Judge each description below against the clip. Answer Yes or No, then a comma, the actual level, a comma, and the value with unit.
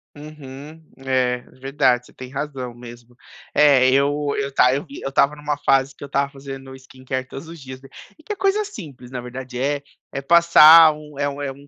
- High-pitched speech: No, medium, 140 Hz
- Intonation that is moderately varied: No, narrow, 2.2 semitones